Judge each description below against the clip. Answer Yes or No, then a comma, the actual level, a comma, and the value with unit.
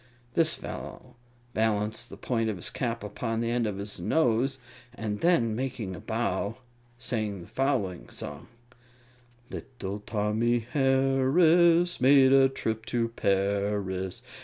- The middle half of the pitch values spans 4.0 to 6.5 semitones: Yes, average, 4.3 semitones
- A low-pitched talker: Yes, low, 115 Hz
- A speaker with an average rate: No, slow, 130 wpm